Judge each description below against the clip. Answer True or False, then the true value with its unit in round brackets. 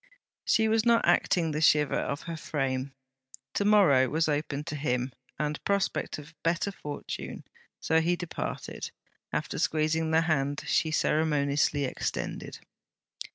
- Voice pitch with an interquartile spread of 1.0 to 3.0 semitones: True (2.7 semitones)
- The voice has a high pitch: False (155 Hz)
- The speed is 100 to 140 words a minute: True (135 wpm)